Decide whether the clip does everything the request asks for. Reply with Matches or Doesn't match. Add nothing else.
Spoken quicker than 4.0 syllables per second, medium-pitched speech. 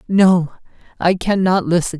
Matches